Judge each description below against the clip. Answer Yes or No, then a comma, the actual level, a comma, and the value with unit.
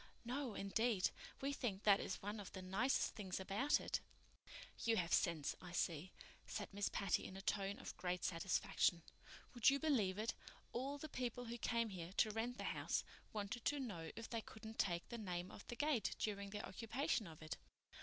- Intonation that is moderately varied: Yes, average, 4.2 semitones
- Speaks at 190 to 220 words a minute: Yes, average, 195 wpm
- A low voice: No, high, 210 Hz